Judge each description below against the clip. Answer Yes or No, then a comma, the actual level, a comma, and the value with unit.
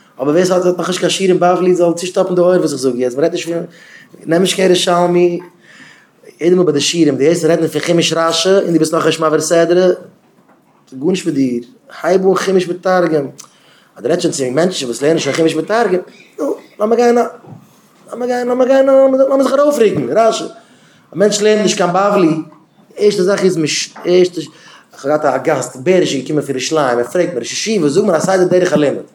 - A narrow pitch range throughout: No, average, 3.2 semitones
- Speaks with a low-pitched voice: No, medium, 175 Hz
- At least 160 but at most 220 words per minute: No, average, 150 wpm